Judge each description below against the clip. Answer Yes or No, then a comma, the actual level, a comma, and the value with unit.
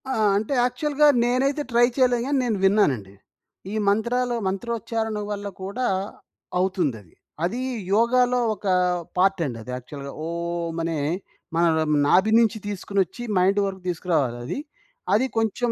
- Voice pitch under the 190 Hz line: No, high, 200 Hz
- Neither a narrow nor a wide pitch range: No, wide, 6.0 semitones